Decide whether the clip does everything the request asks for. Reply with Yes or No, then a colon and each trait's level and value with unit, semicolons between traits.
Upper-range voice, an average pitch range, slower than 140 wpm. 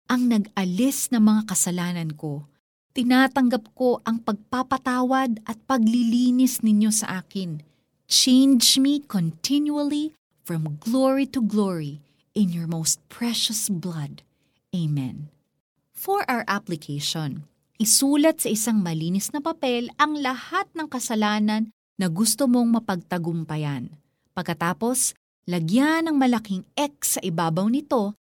No: high, 220 Hz; wide, 6.5 semitones; slow, 110 wpm